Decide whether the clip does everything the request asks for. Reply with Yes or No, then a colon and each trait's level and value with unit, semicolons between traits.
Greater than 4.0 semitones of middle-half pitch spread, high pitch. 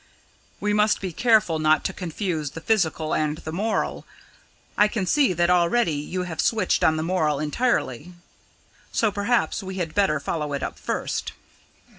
No: average, 4.9 semitones; medium, 180 Hz